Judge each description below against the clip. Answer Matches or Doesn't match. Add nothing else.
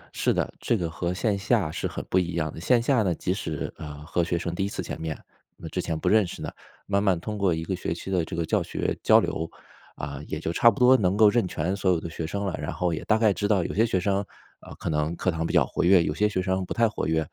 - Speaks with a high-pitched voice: Doesn't match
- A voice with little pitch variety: Doesn't match